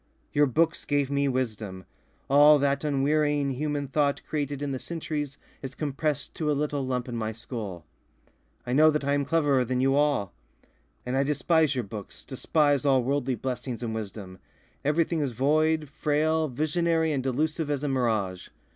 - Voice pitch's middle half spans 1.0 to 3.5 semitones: Yes, average, 3.0 semitones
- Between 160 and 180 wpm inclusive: Yes, average, 170 wpm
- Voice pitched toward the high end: No, medium, 140 Hz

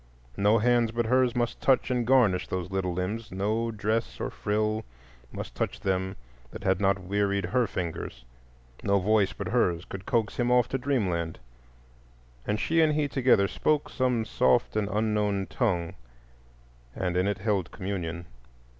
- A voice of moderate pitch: No, low, 105 Hz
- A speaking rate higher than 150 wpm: Yes, average, 160 wpm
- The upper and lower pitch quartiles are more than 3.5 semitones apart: Yes, average, 4.0 semitones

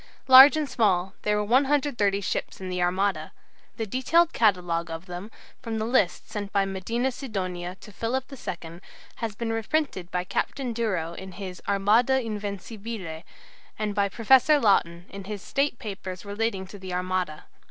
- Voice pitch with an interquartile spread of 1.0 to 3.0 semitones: No, average, 4.1 semitones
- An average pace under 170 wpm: Yes, average, 160 wpm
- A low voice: No, high, 205 Hz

